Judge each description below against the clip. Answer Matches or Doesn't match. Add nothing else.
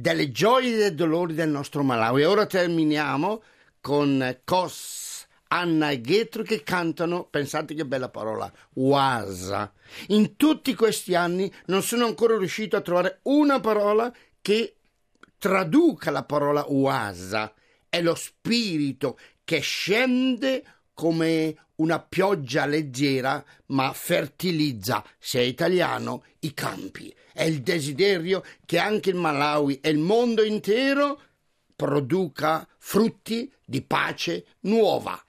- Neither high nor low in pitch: Matches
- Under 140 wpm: Matches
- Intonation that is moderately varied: Doesn't match